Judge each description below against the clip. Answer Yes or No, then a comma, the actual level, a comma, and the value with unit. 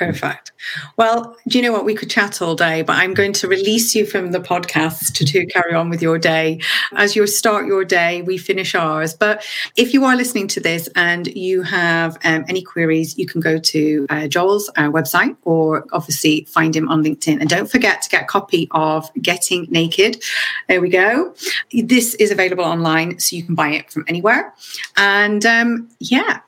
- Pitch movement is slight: No, average, 4.4 semitones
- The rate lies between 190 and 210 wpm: Yes, average, 200 wpm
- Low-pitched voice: No, medium, 175 Hz